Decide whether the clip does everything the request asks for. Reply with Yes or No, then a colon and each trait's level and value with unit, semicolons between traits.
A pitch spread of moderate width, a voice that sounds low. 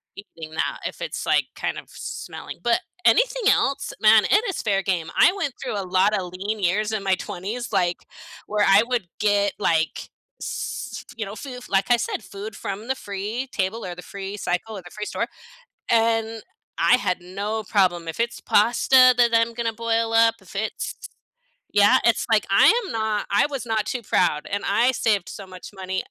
No: average, 3.1 semitones; high, 210 Hz